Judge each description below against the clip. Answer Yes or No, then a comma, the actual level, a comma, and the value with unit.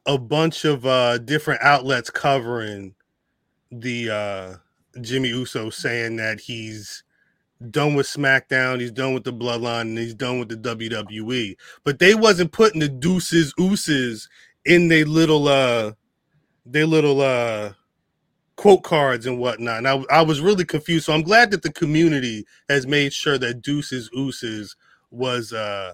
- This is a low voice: Yes, low, 130 Hz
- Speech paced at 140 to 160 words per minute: Yes, average, 155 wpm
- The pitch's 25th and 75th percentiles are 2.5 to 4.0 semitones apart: No, average, 4.6 semitones